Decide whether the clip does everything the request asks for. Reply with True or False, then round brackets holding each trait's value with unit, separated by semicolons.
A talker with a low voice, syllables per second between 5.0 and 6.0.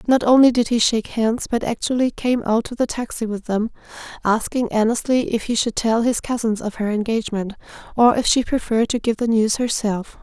False (230 Hz; 5.5 syllables/s)